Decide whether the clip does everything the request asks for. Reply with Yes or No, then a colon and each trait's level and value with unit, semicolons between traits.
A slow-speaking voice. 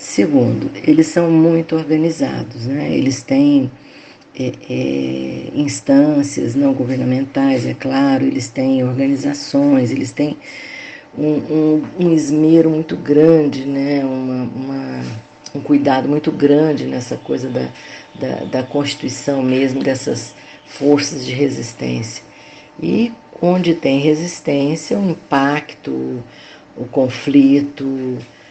Yes: slow, 115 wpm